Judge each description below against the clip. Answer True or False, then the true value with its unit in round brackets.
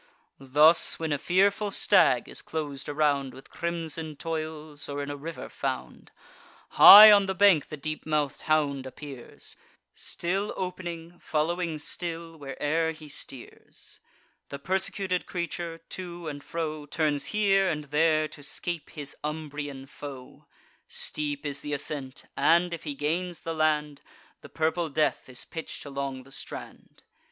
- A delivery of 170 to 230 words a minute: False (145 wpm)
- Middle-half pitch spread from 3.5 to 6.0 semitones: False (2.8 semitones)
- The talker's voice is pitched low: False (155 Hz)